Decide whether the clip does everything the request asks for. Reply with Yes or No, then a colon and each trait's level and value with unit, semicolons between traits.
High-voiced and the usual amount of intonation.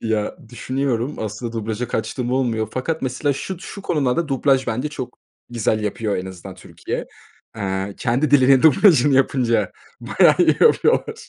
No: low, 125 Hz; average, 3.9 semitones